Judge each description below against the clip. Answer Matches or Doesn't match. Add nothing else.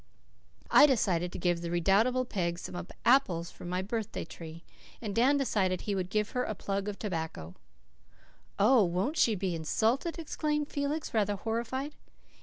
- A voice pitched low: Doesn't match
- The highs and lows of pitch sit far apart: Matches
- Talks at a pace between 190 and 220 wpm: Doesn't match